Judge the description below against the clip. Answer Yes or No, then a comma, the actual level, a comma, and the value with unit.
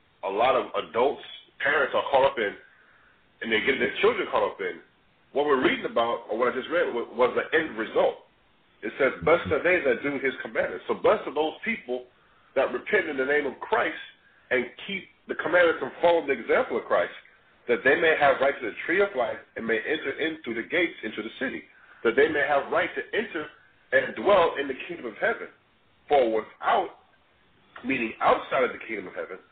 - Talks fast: Yes, fast, 210 wpm